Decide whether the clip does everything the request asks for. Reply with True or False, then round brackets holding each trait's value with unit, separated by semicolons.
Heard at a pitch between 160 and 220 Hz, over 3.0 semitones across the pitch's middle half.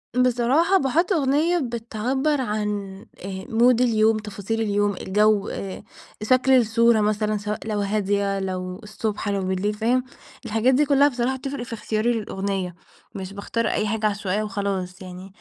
True (215 Hz; 3.5 semitones)